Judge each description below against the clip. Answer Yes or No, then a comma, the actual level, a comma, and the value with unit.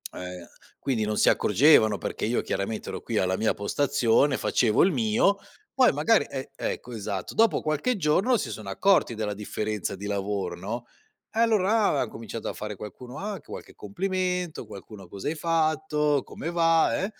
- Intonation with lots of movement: Yes, wide, 8.2 semitones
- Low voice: Yes, low, 125 Hz